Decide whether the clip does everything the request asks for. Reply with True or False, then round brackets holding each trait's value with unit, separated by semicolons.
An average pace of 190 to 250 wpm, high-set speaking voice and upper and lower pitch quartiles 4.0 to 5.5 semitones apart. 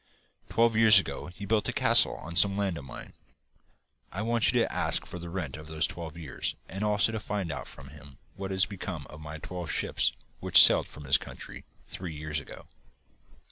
False (205 wpm; 90 Hz; 4.7 semitones)